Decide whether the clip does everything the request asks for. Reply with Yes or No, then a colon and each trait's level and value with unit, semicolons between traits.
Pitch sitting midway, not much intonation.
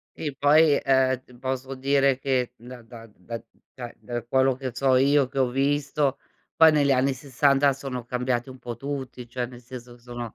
No: low, 130 Hz; narrow, 2.1 semitones